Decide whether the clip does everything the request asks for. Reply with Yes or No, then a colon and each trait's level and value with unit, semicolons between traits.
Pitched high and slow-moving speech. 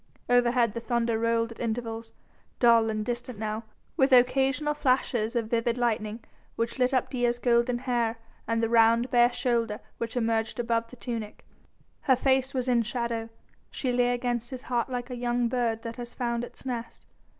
No: high, 240 Hz; average, 175 wpm